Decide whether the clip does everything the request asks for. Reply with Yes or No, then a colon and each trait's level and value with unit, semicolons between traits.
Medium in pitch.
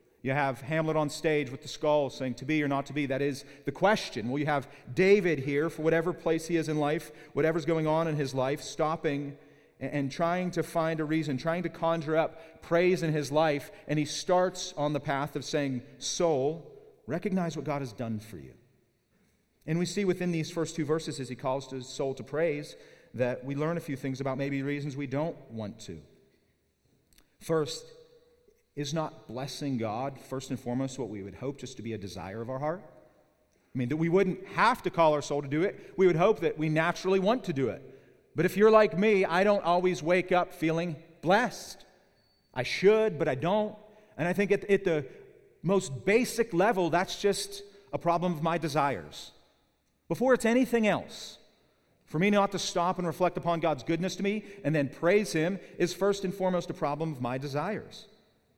Yes: medium, 160 Hz